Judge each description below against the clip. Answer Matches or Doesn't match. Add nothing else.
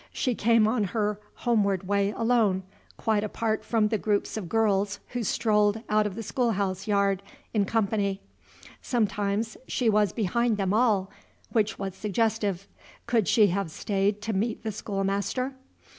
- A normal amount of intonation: Doesn't match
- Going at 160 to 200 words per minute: Doesn't match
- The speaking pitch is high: Matches